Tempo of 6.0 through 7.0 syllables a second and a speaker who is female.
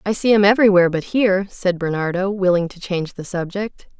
Yes: 6.2 syllables/s; female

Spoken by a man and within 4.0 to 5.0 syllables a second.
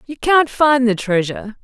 No: female; 4.7 syllables/s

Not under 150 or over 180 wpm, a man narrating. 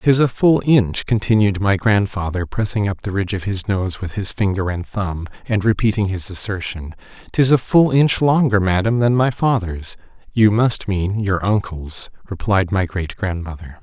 Yes: average, 170 wpm; male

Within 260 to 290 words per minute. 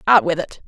Yes: fast, 270 wpm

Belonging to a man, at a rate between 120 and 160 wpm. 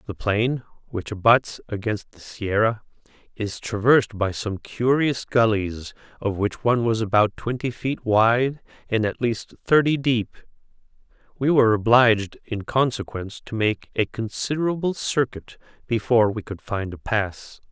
Yes: male; average, 140 wpm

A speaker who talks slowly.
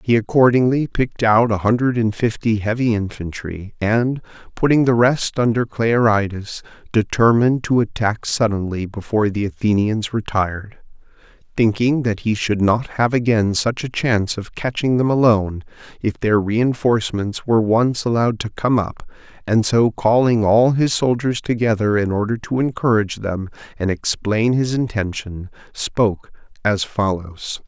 No: average, 145 wpm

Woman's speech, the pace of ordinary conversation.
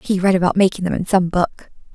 No: female; fast, 245 wpm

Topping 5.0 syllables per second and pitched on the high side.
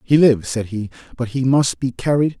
No: 5.5 syllables/s; low, 120 Hz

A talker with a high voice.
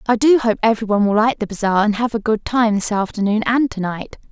Yes: high, 220 Hz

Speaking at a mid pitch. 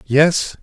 Yes: medium, 150 Hz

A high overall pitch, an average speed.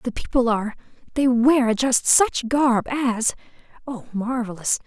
No: high, 245 Hz; slow, 110 wpm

